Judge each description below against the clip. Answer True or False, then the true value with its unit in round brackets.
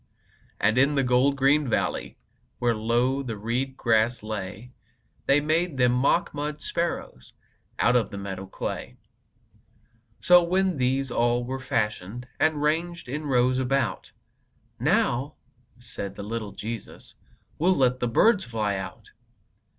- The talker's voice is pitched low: True (125 Hz)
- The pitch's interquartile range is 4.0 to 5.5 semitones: True (4.3 semitones)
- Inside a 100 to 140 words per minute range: True (135 wpm)